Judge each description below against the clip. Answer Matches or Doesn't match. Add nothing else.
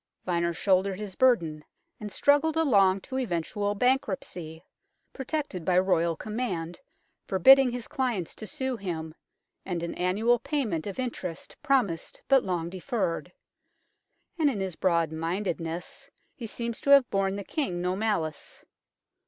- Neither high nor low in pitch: Doesn't match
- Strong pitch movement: Matches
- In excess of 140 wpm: Doesn't match